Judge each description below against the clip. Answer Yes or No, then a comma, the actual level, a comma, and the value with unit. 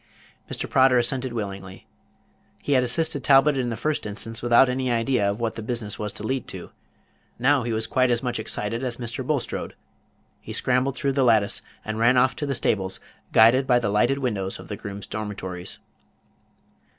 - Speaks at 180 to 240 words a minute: Yes, average, 185 wpm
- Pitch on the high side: No, low, 120 Hz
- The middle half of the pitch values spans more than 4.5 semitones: No, average, 3.4 semitones